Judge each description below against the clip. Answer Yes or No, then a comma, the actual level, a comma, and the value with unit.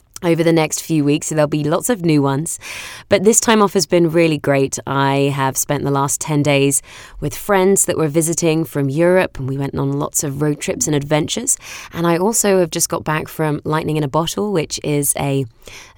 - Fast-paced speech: Yes, fast, 220 wpm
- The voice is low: No, medium, 155 Hz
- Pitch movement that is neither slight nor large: Yes, average, 3.3 semitones